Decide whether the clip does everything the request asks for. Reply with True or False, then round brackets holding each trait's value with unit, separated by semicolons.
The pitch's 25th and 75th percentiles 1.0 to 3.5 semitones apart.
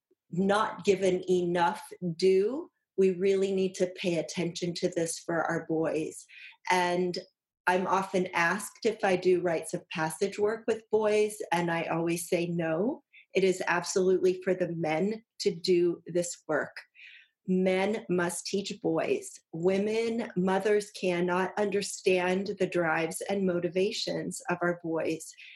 True (2.5 semitones)